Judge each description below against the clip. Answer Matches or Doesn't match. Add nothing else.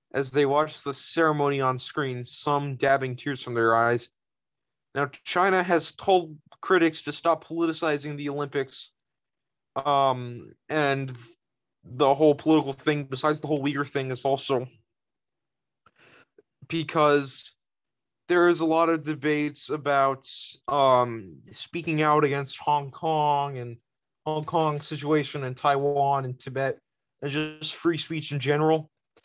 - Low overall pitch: Doesn't match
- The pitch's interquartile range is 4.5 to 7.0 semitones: Doesn't match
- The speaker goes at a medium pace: Doesn't match